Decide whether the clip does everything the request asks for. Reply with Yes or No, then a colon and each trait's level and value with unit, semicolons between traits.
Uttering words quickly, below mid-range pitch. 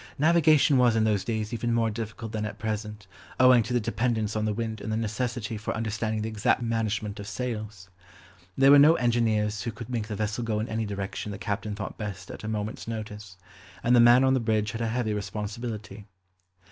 Yes: fast, 210 wpm; low, 110 Hz